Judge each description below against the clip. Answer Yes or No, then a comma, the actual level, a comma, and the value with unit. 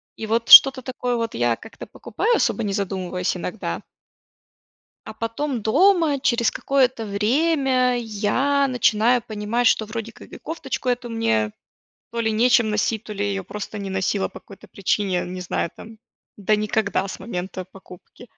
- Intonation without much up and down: No, average, 3.8 semitones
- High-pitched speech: Yes, high, 220 Hz